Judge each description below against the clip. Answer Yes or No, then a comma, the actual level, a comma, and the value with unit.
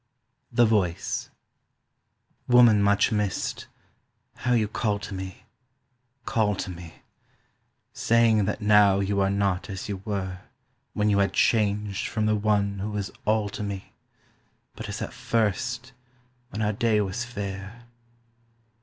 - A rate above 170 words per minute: No, slow, 135 wpm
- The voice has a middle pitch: No, low, 105 Hz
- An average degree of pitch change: No, narrow, 1.7 semitones